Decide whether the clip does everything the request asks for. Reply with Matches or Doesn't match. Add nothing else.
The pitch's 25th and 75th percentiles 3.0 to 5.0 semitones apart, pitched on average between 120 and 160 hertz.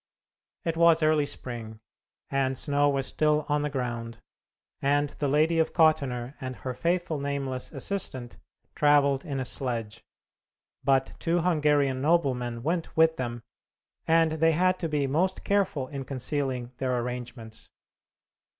Matches